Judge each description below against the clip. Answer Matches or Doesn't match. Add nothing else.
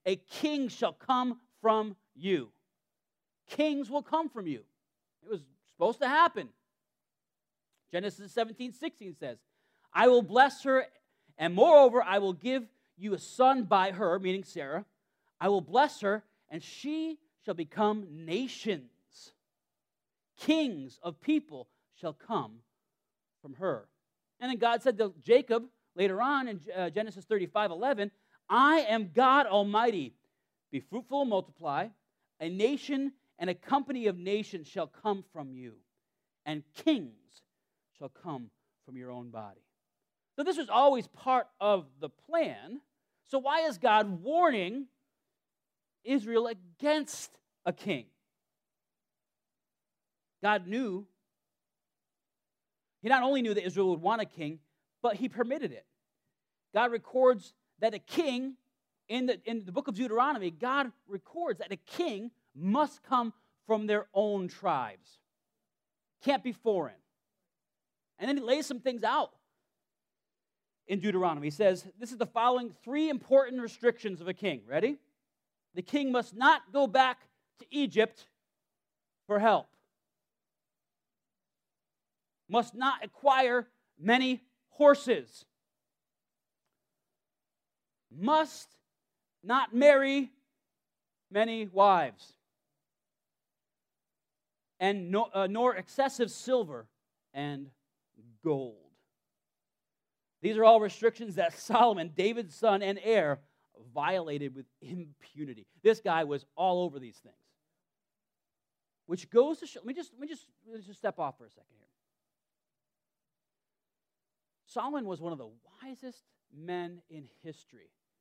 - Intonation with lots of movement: Matches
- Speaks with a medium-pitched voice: Doesn't match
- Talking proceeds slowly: Matches